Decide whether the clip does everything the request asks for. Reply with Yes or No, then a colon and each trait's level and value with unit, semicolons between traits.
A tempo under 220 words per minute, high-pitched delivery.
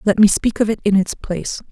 No: fast, 280 wpm; high, 205 Hz